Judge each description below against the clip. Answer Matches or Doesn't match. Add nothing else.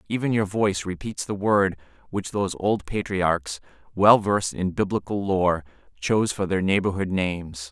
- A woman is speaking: Doesn't match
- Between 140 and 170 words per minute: Matches